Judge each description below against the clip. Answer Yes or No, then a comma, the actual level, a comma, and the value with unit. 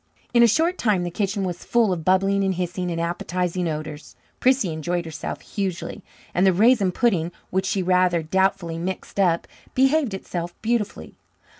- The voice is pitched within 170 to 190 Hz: Yes, medium, 185 Hz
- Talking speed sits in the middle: Yes, average, 165 wpm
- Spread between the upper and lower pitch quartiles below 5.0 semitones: Yes, average, 2.8 semitones